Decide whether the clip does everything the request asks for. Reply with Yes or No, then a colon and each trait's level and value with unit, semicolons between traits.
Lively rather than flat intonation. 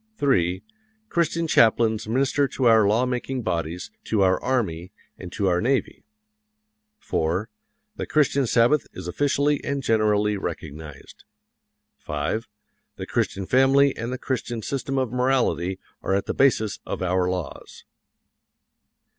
Yes: wide, 6.3 semitones